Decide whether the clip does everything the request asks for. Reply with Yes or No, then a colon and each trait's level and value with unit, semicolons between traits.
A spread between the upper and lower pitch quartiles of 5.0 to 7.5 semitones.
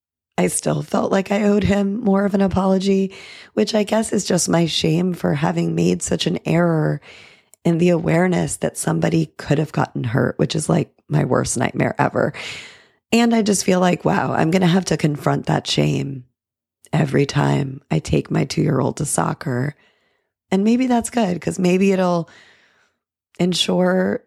Yes: wide, 5.5 semitones